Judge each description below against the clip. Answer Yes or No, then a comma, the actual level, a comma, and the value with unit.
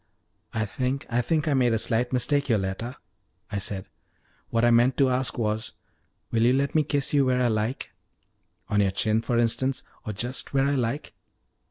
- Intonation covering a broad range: No, average, 3.2 semitones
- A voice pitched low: Yes, low, 120 Hz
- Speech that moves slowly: No, average, 190 wpm